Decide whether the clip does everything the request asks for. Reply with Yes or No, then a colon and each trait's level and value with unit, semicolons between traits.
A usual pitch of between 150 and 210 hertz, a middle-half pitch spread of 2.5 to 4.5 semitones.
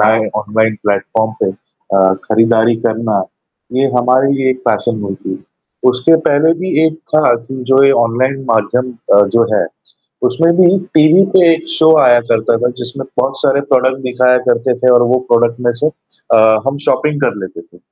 No: low, 125 Hz; average, 3.4 semitones